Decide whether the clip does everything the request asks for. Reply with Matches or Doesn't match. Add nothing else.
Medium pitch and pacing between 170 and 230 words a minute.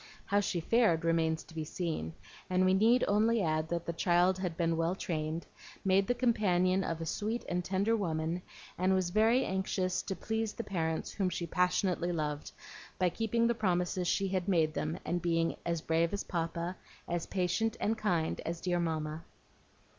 Matches